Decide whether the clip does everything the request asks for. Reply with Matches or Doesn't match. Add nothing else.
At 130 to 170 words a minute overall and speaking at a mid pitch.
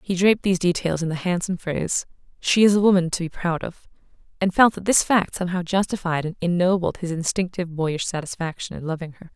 Doesn't match